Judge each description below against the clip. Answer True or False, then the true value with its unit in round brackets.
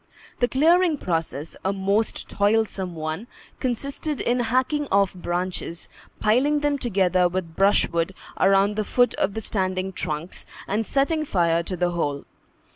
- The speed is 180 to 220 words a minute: False (140 wpm)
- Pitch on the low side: False (195 Hz)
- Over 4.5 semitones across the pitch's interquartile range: True (5.6 semitones)